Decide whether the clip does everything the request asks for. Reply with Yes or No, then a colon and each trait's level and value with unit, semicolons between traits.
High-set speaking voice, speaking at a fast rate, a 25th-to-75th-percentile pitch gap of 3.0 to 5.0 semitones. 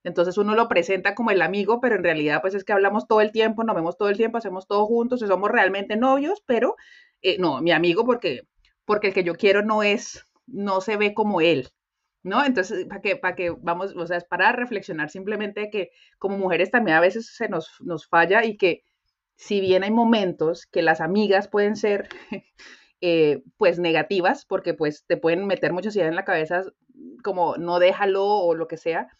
Yes: high, 195 Hz; fast, 205 wpm; average, 3.6 semitones